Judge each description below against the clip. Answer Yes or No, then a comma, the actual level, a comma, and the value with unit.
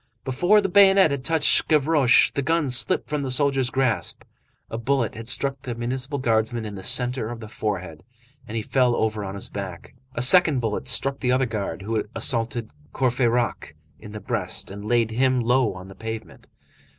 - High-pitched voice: No, low, 120 Hz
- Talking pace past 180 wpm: Yes, average, 190 wpm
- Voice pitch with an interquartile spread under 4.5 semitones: Yes, average, 3.5 semitones